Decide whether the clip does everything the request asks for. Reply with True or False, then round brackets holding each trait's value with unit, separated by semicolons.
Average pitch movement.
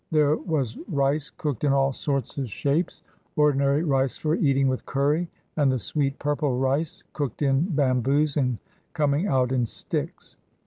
False (2.0 semitones)